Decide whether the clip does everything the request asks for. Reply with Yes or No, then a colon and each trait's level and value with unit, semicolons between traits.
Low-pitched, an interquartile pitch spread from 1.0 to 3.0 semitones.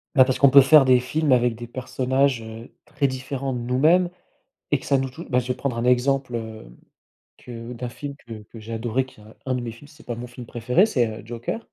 Yes: low, 125 Hz; narrow, 2.6 semitones